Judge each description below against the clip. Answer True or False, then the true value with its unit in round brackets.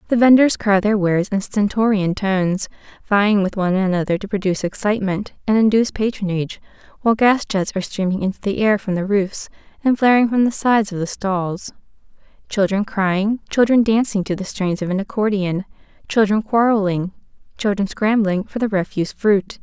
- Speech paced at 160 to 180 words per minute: True (170 wpm)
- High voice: True (205 Hz)